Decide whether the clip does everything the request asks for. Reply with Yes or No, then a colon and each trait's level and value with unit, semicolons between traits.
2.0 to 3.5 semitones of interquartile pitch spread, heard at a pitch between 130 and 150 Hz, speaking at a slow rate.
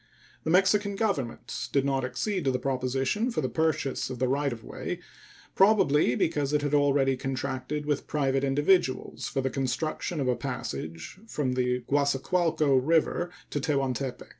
No: average, 3.2 semitones; medium, 140 Hz; average, 160 wpm